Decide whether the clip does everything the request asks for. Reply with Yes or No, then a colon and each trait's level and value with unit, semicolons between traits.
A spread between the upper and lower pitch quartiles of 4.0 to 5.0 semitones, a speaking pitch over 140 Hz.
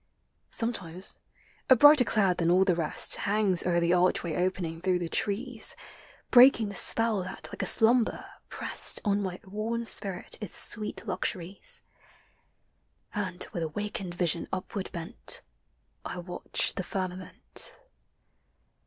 No: average, 3.3 semitones; high, 190 Hz